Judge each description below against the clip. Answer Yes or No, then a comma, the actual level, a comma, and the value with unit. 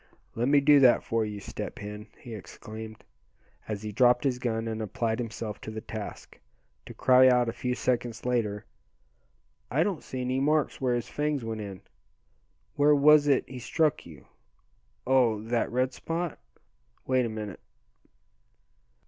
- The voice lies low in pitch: Yes, low, 120 Hz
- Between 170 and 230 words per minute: No, average, 160 wpm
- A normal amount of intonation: Yes, average, 3.3 semitones